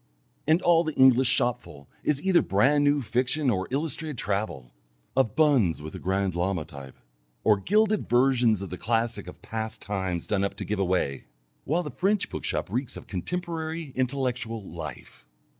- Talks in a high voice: No, low, 120 Hz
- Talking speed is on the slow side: No, average, 165 wpm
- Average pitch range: No, wide, 7.1 semitones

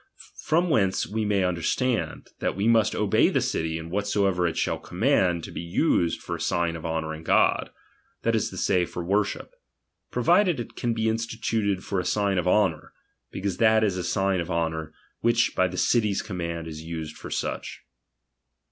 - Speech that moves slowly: No, average, 185 wpm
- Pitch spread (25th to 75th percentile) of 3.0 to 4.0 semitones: No, average, 4.4 semitones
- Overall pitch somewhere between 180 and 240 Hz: No, very low, 95 Hz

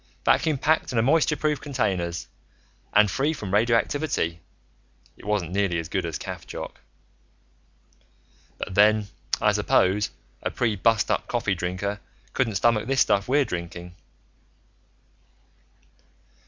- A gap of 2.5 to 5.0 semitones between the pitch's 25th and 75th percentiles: No, wide, 5.5 semitones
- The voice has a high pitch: No, low, 105 Hz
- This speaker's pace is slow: Yes, slow, 115 wpm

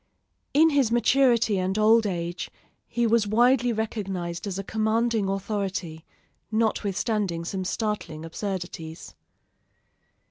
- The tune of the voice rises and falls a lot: No, average, 3.7 semitones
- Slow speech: Yes, slow, 105 wpm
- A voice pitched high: Yes, high, 210 Hz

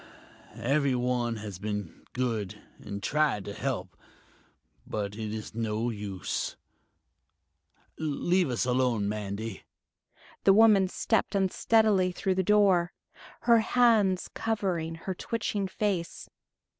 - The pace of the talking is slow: Yes, slow, 105 wpm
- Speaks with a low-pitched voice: No, medium, 145 Hz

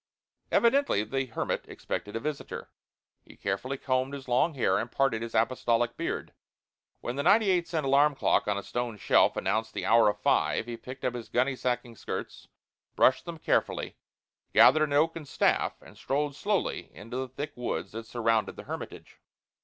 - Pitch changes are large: No, average, 3.9 semitones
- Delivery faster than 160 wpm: Yes, average, 175 wpm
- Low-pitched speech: Yes, low, 130 Hz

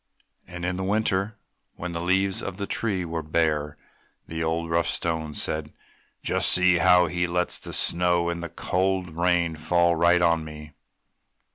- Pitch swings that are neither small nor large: No, narrow, 1.7 semitones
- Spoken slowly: No, average, 170 wpm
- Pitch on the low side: Yes, very low, 85 Hz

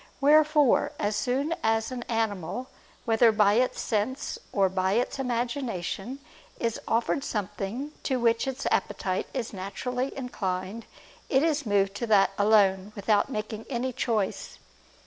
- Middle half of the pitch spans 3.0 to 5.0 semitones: Yes, average, 4.1 semitones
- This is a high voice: Yes, high, 225 Hz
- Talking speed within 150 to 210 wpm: No, slow, 135 wpm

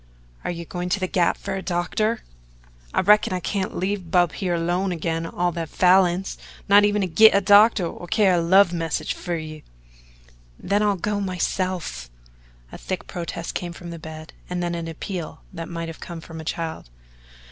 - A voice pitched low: No, medium, 175 Hz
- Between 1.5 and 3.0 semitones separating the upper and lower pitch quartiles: Yes, narrow, 2.5 semitones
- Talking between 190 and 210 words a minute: Yes, average, 195 wpm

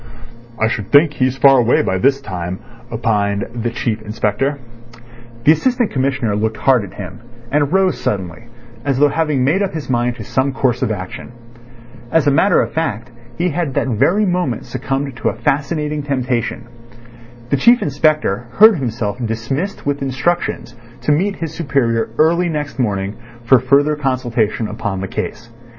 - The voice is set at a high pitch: No, low, 130 Hz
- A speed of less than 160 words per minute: No, average, 165 wpm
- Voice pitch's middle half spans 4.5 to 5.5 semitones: Yes, average, 4.8 semitones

